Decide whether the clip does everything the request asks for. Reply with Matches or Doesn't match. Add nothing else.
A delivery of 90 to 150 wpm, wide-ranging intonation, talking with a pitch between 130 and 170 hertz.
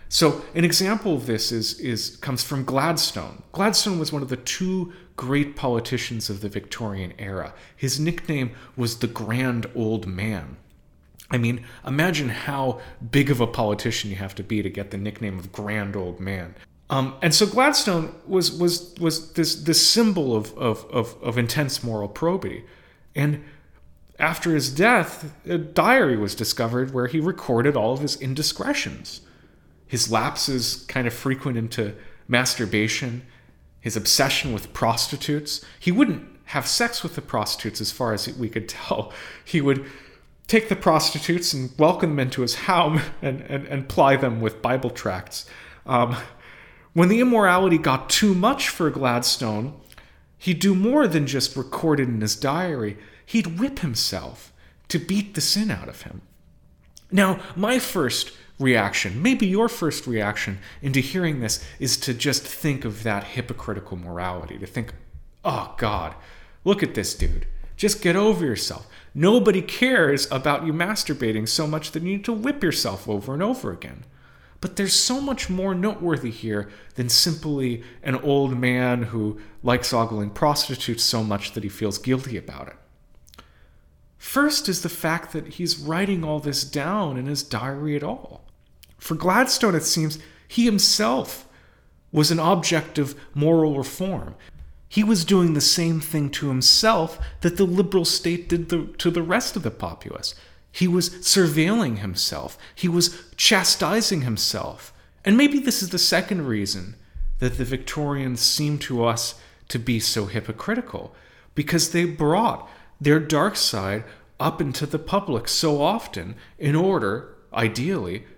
Doesn't match